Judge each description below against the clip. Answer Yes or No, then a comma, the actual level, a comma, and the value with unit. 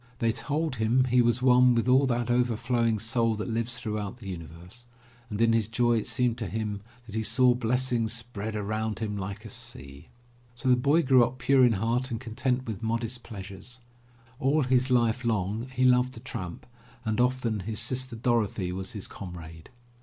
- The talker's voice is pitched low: Yes, low, 115 Hz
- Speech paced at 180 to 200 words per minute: Yes, average, 190 wpm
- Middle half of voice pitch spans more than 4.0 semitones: No, average, 2.7 semitones